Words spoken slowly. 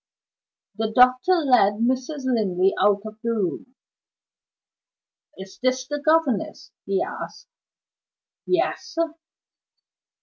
Yes: slow, 95 wpm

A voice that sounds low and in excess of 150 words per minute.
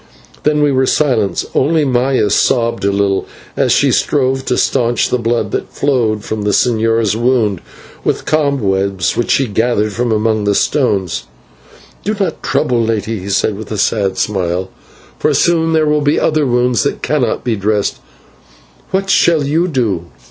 Yes: low, 120 Hz; average, 165 wpm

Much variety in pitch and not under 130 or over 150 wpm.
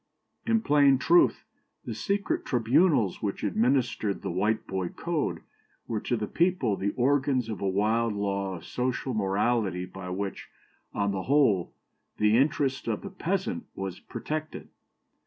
Yes: wide, 6.4 semitones; average, 140 wpm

